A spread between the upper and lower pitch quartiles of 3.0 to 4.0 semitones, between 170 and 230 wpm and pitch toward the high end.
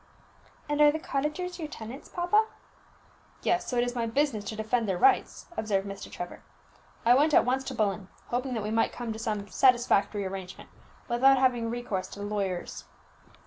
No: average, 4.8 semitones; average, 185 wpm; high, 235 Hz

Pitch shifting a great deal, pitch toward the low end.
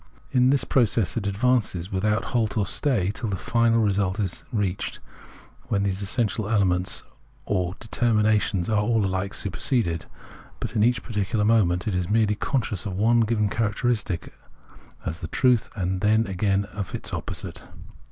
No: average, 3.1 semitones; low, 105 Hz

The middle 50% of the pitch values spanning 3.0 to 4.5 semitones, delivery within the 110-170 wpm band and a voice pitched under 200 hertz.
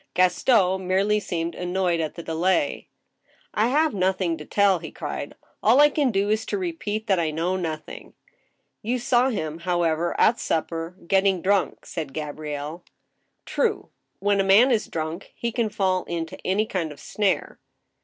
No: average, 4.2 semitones; average, 180 wpm; medium, 185 Hz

